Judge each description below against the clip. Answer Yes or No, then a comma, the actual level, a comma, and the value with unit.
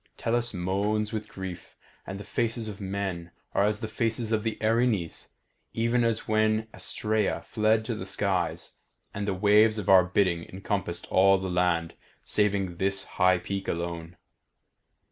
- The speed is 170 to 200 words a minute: No, average, 155 wpm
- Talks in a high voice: No, low, 100 Hz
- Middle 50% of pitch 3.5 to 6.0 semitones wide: No, average, 2.8 semitones